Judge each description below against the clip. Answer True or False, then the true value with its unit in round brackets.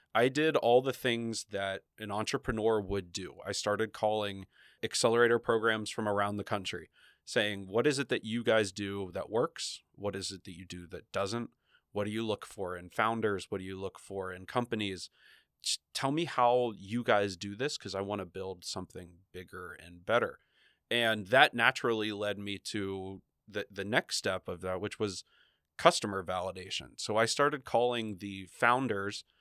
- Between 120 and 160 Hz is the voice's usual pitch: False (105 Hz)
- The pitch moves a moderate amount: True (3.0 semitones)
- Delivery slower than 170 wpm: False (185 wpm)